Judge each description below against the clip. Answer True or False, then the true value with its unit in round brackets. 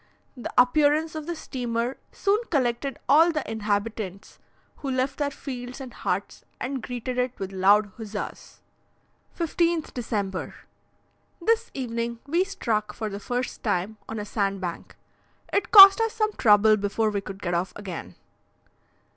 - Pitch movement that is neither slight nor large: False (5.9 semitones)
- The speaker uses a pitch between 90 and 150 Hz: False (240 Hz)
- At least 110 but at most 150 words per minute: True (145 wpm)